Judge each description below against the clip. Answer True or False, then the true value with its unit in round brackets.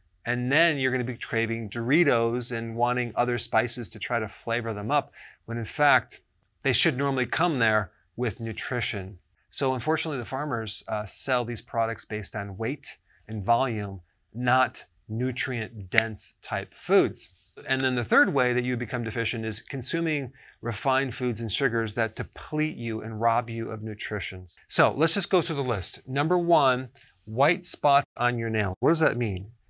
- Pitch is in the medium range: False (120 Hz)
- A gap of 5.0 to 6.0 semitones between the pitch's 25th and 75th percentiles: False (3.0 semitones)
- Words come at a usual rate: True (175 wpm)